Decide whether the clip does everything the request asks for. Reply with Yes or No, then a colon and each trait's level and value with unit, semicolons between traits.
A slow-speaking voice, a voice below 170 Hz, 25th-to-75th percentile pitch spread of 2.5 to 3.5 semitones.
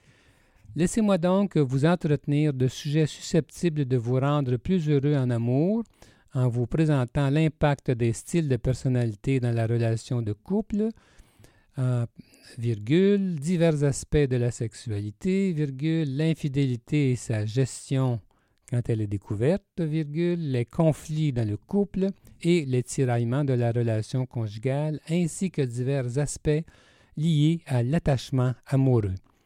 No: slow, 130 wpm; medium, 140 Hz; average, 4.7 semitones